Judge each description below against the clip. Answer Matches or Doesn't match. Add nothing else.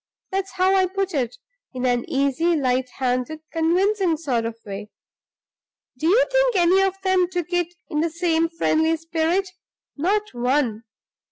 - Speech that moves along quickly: Doesn't match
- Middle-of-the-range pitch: Doesn't match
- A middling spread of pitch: Doesn't match